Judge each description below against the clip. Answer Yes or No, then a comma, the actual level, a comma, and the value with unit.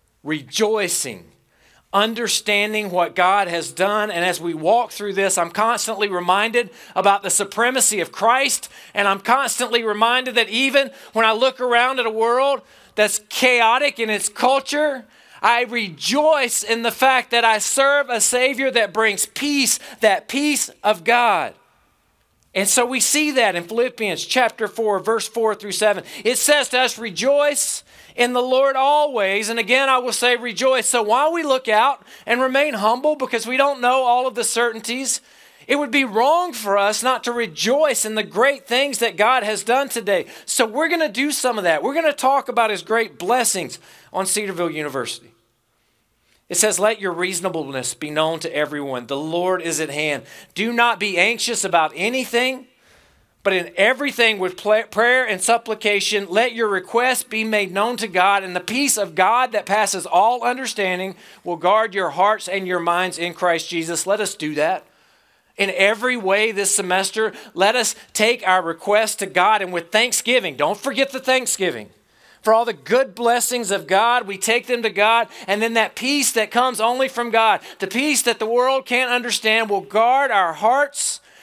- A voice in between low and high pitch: No, high, 225 Hz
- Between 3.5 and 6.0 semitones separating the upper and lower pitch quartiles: Yes, average, 4.3 semitones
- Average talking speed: Yes, average, 180 wpm